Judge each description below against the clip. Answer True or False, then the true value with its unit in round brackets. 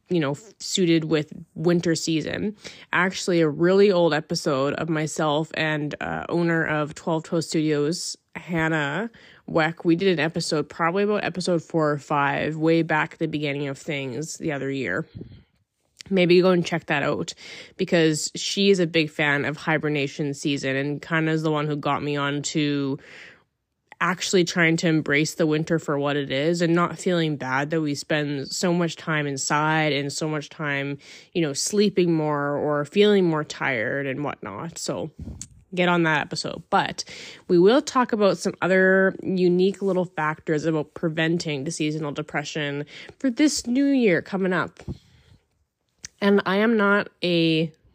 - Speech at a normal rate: True (165 wpm)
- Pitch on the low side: False (160 Hz)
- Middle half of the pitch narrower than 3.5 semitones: True (3.1 semitones)